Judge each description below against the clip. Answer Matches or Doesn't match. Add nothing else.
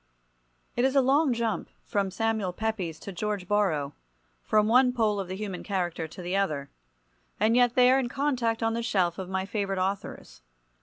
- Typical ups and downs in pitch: Matches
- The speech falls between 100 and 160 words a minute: Doesn't match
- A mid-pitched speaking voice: Doesn't match